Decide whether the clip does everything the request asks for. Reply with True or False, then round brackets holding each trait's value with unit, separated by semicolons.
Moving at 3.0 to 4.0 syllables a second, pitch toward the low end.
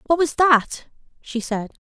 False (3.8 syllables/s; 275 Hz)